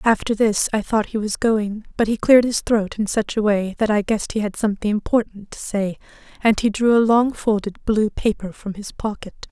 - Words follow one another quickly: Yes, fast, 225 wpm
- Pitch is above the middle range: Yes, high, 215 Hz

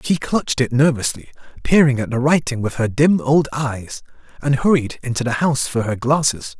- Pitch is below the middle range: Yes, low, 130 Hz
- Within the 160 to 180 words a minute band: No, average, 190 wpm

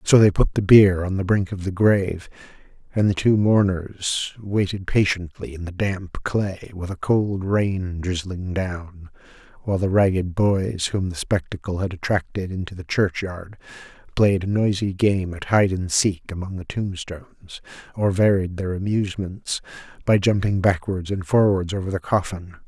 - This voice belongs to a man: Yes, male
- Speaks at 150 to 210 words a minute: Yes, average, 165 wpm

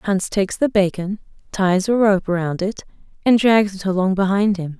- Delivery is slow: No, average, 190 wpm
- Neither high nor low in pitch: No, high, 195 Hz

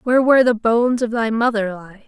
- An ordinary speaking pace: No, fast, 230 wpm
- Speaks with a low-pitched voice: No, high, 230 Hz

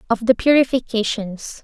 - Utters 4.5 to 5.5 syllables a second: Yes, 4.9 syllables/s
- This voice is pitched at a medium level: No, high, 235 Hz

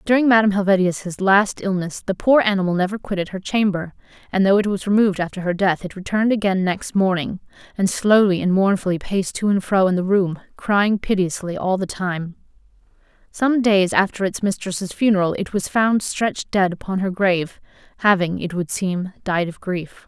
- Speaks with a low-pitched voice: No, high, 190 Hz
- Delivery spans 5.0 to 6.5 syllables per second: Yes, 5.4 syllables/s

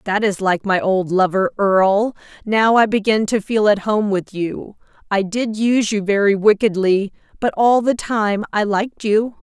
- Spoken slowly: No, average, 185 wpm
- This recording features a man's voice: No, female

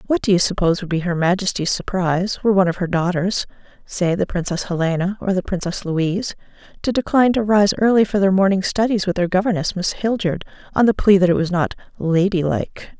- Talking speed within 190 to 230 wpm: Yes, average, 200 wpm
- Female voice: Yes, female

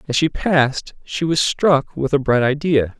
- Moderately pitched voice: Yes, medium, 145 Hz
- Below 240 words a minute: Yes, average, 200 wpm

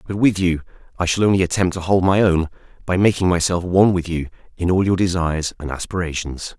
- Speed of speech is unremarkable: No, fast, 210 wpm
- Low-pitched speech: Yes, very low, 90 Hz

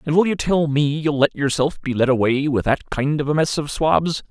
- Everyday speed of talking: No, fast, 265 wpm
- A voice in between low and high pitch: Yes, medium, 145 Hz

